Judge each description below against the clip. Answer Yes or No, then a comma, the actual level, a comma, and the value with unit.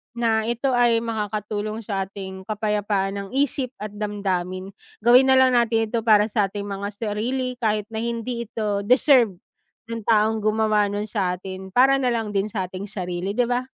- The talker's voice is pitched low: No, high, 215 Hz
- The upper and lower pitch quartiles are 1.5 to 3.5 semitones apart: Yes, average, 2.7 semitones